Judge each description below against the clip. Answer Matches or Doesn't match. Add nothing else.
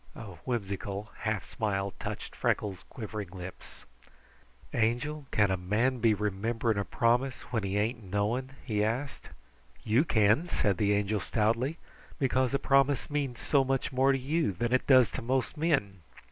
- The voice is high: Doesn't match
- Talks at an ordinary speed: Matches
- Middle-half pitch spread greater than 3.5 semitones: Matches